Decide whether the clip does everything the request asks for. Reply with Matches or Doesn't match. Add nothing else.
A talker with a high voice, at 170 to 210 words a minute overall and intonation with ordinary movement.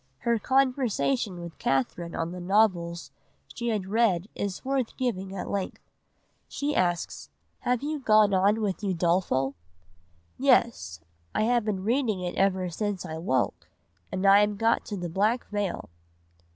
Doesn't match